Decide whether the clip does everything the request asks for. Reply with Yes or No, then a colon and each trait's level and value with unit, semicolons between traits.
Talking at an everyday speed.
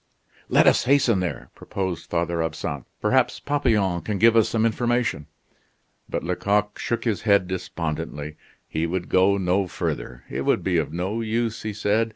Yes: average, 165 wpm